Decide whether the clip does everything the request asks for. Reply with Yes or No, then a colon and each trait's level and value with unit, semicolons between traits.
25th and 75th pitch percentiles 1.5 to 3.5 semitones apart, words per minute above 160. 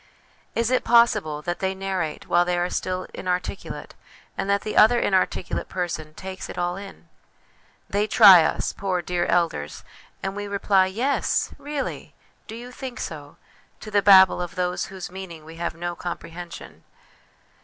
Yes: narrow, 2.5 semitones; average, 170 wpm